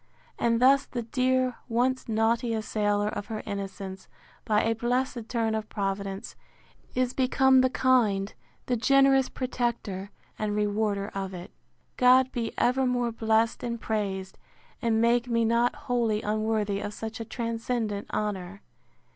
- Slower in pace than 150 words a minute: Yes, average, 140 wpm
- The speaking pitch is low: No, high, 225 Hz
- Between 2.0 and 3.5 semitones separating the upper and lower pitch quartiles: Yes, average, 3.0 semitones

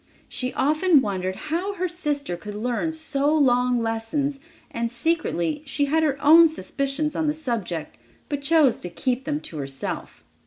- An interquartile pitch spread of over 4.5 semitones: Yes, average, 5.3 semitones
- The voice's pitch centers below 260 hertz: No, very high, 275 Hz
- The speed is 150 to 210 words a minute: Yes, average, 160 wpm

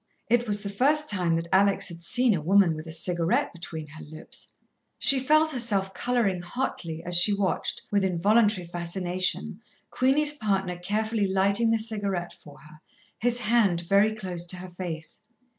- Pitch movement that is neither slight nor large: Yes, average, 4.2 semitones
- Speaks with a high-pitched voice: Yes, high, 195 Hz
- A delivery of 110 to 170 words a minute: Yes, average, 165 wpm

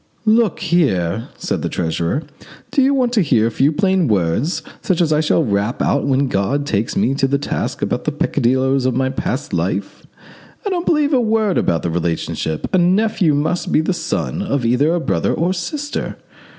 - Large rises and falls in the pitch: Yes, wide, 8.4 semitones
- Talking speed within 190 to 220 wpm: Yes, average, 195 wpm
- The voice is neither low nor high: Yes, medium, 145 Hz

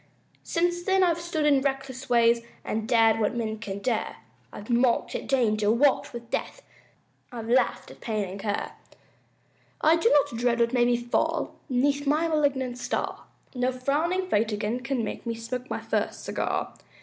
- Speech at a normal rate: Yes, average, 170 wpm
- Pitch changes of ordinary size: Yes, average, 3.8 semitones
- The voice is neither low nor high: No, high, 245 Hz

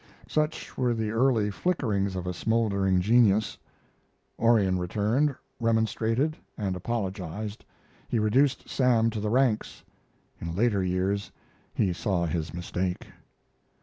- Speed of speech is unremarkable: No, slow, 115 wpm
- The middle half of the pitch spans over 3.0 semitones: Yes, average, 3.8 semitones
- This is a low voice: Yes, low, 105 Hz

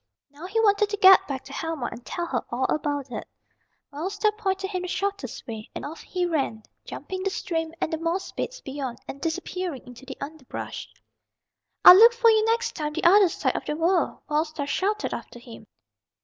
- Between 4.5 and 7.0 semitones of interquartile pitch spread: Yes, average, 5.3 semitones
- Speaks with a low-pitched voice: No, very high, 330 Hz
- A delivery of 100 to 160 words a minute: No, fast, 205 wpm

